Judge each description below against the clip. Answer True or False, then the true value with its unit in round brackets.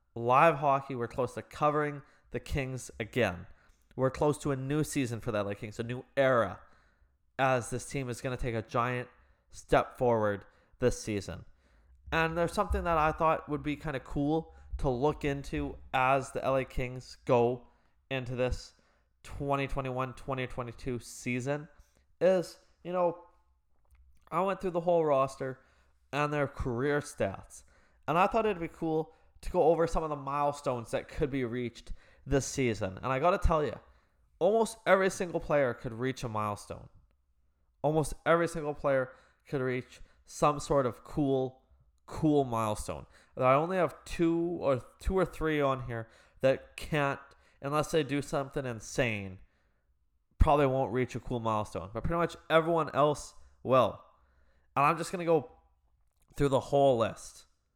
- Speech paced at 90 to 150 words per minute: False (160 wpm)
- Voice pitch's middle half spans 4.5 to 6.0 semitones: True (4.9 semitones)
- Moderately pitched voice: False (130 Hz)